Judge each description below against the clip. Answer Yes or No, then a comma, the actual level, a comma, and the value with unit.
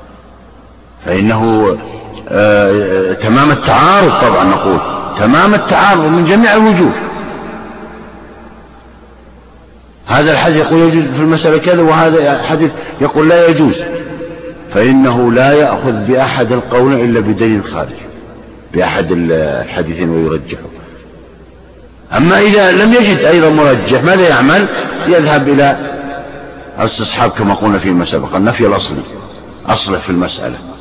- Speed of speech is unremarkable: Yes, average, 110 wpm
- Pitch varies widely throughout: Yes, wide, 8.8 semitones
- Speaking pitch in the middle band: No, low, 130 Hz